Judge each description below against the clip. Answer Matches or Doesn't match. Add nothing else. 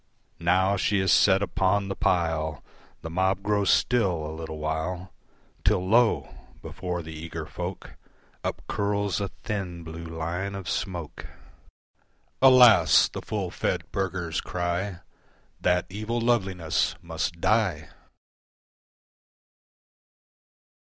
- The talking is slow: Matches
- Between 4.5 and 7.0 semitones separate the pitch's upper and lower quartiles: Doesn't match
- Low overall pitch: Matches